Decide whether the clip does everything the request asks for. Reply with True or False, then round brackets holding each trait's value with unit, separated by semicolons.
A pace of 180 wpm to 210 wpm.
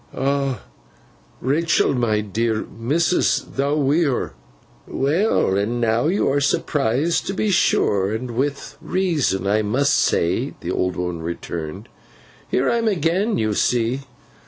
False (135 wpm)